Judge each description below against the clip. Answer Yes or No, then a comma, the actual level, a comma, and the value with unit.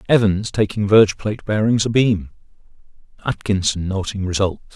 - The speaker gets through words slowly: Yes, slow, 115 wpm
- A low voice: Yes, low, 105 Hz